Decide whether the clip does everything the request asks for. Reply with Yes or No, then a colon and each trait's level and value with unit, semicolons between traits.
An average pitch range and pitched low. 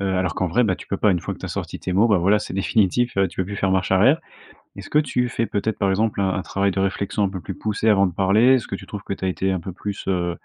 No: narrow, 2.2 semitones; low, 100 Hz